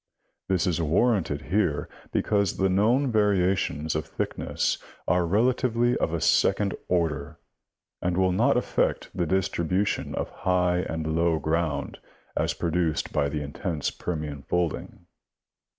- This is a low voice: Yes, very low, 90 Hz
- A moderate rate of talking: No, slow, 130 wpm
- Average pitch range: Yes, average, 3.5 semitones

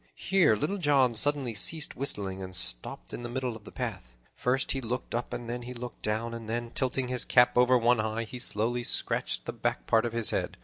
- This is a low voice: Yes, low, 120 Hz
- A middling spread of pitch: No, narrow, 2.2 semitones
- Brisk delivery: Yes, fast, 225 wpm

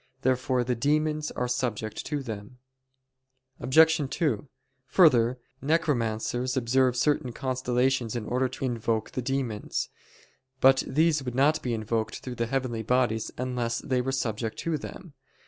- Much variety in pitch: No, narrow, 2.5 semitones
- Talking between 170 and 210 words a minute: No, average, 140 wpm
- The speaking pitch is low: Yes, low, 125 Hz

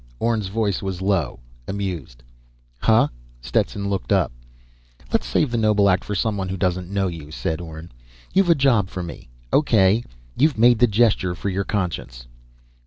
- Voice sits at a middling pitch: No, low, 100 Hz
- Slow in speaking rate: No, average, 165 wpm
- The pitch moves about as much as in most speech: Yes, average, 3.8 semitones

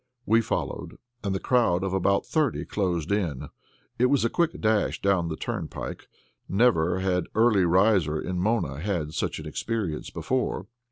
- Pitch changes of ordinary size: Yes, average, 4.5 semitones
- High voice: No, very low, 95 Hz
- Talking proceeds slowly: No, average, 160 wpm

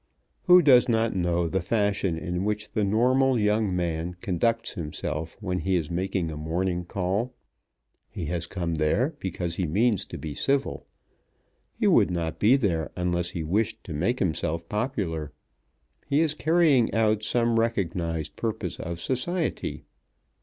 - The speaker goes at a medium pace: Yes, average, 155 wpm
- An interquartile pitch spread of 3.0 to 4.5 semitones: No, average, 5.3 semitones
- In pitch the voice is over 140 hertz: No, very low, 95 Hz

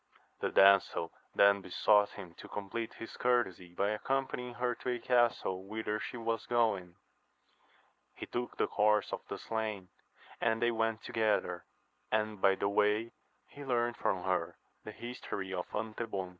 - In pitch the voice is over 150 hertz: No, low, 110 Hz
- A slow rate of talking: No, average, 155 wpm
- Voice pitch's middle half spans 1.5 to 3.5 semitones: Yes, average, 3.2 semitones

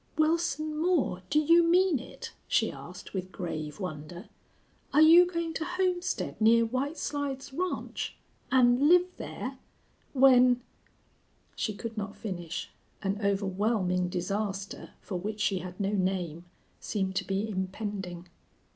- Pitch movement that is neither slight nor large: No, wide, 8.3 semitones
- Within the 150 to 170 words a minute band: No, slow, 135 wpm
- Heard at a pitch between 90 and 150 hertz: No, high, 215 Hz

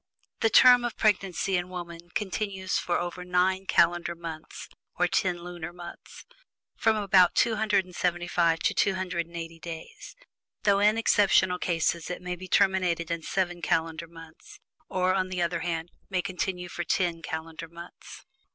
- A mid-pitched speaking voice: Yes, medium, 180 Hz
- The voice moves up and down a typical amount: No, narrow, 1.9 semitones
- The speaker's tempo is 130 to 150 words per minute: Yes, average, 145 wpm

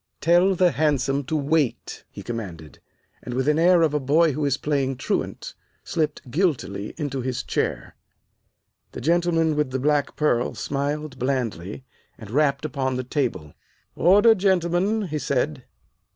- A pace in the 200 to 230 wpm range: No, average, 150 wpm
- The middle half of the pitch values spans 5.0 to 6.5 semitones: No, average, 4.1 semitones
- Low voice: No, medium, 145 Hz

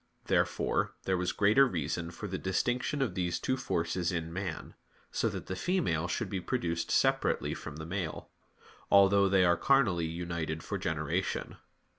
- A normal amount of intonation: Yes, average, 3.1 semitones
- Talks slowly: No, average, 160 wpm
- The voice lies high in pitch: No, very low, 90 Hz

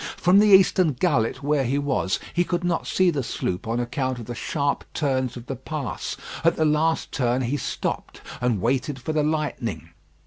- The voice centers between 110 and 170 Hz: Yes, medium, 140 Hz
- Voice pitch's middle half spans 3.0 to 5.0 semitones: Yes, average, 4.4 semitones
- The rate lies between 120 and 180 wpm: No, average, 195 wpm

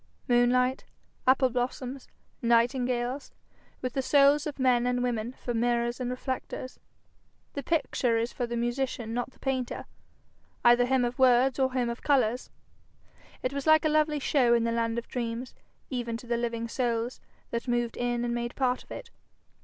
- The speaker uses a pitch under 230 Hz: No, high, 245 Hz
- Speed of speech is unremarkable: Yes, average, 170 wpm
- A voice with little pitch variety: Yes, narrow, 1.7 semitones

